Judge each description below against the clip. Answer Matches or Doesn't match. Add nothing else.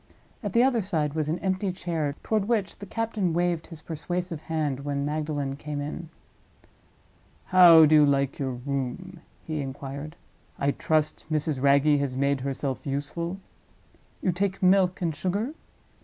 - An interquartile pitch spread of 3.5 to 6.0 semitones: Matches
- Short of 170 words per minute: Matches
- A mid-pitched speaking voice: Matches